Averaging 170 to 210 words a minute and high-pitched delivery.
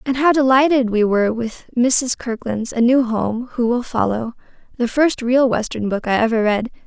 Yes: average, 185 wpm; high, 240 Hz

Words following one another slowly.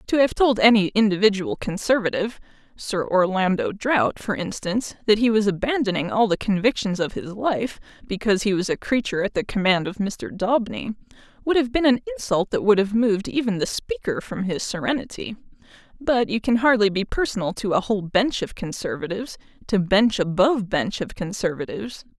No: average, 170 wpm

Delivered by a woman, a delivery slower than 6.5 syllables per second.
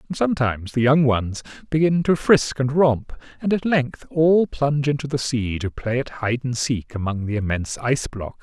No: male; 5.0 syllables/s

